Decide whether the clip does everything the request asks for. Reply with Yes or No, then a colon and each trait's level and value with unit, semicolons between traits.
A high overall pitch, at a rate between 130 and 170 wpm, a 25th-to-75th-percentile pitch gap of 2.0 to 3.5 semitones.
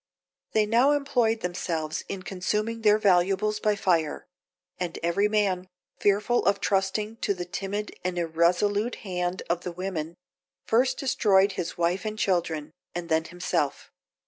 Yes: high, 195 Hz; average, 145 wpm; average, 3.2 semitones